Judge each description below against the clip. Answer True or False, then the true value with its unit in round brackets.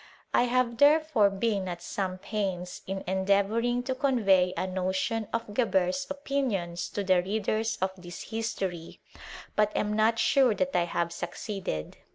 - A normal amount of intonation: True (3.9 semitones)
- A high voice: True (205 Hz)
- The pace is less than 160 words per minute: True (150 wpm)